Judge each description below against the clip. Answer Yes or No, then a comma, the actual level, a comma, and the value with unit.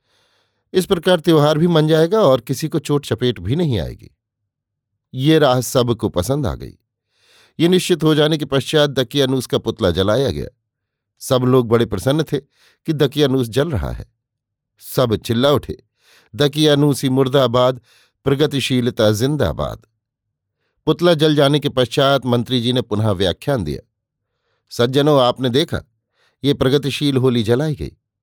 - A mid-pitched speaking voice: No, low, 130 Hz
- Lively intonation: No, average, 3.9 semitones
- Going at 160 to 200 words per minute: No, average, 145 wpm